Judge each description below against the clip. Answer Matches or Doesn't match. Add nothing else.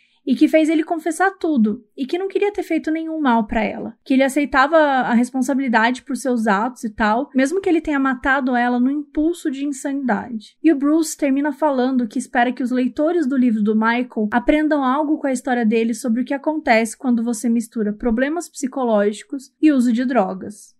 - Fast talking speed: Matches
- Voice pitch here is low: Doesn't match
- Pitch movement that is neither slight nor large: Matches